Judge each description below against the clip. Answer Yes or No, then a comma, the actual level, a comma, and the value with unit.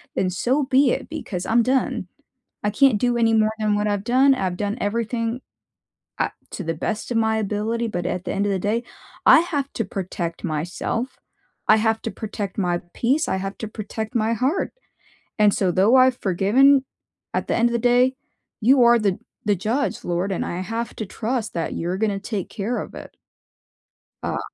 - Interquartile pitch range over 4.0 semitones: No, average, 3.7 semitones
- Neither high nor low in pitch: No, high, 220 Hz